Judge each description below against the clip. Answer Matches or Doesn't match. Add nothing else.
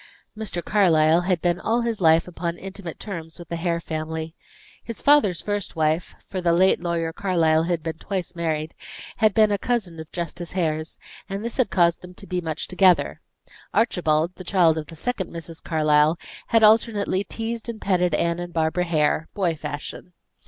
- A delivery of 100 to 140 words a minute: Doesn't match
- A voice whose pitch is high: Doesn't match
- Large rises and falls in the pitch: Doesn't match